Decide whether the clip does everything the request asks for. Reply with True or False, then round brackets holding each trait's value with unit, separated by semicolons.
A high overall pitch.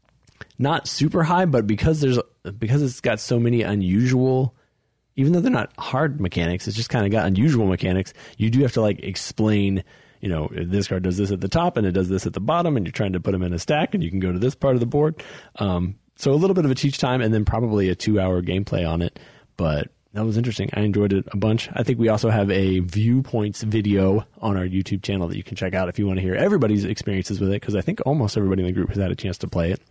False (105 Hz)